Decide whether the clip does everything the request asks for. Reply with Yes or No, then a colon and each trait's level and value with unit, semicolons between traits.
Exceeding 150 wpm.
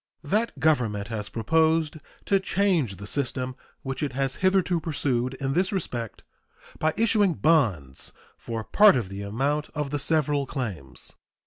No: average, 145 wpm